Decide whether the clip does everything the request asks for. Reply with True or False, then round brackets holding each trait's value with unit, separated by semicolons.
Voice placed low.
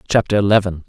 True (100 Hz)